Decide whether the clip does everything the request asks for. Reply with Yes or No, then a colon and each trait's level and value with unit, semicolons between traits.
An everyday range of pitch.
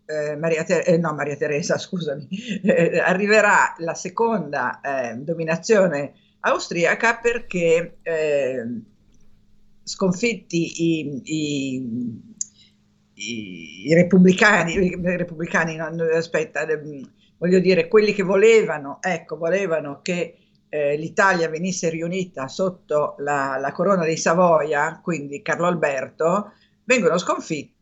Yes: average, 4.1 semitones